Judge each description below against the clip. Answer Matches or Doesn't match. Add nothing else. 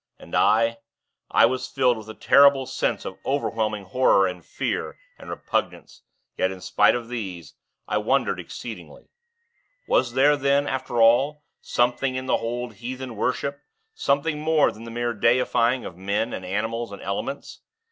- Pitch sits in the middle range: Doesn't match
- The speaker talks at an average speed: Matches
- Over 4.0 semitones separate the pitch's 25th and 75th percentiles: Doesn't match